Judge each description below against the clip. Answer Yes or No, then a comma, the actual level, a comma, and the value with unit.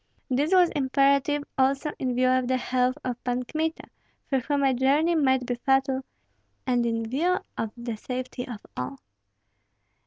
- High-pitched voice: Yes, very high, 260 Hz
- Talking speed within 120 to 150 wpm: No, average, 160 wpm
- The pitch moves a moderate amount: No, narrow, 2.1 semitones